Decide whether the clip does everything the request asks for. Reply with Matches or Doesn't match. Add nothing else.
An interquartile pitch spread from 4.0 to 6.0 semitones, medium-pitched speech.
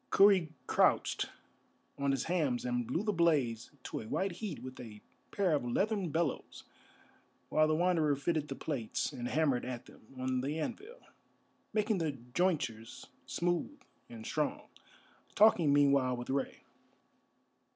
Matches